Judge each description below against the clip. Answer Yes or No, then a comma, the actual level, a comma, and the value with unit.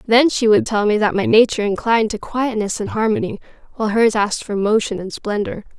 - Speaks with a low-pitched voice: No, high, 215 Hz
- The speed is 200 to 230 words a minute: Yes, fast, 205 wpm